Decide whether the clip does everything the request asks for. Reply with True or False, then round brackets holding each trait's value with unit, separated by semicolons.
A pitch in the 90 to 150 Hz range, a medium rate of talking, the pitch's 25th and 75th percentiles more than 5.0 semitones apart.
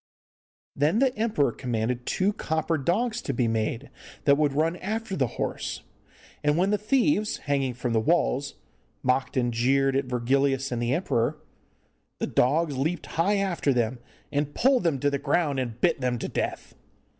True (140 Hz; 170 wpm; 5.6 semitones)